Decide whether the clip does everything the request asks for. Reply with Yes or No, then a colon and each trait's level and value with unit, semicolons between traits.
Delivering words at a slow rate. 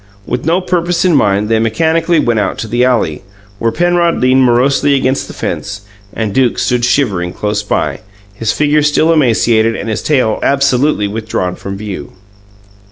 No: average, 165 wpm